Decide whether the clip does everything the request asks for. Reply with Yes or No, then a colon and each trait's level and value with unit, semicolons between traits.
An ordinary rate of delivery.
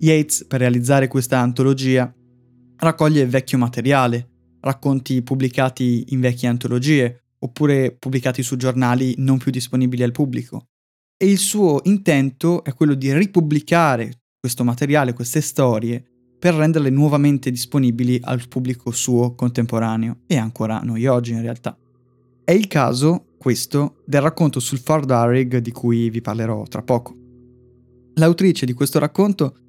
Yes: average, 135 wpm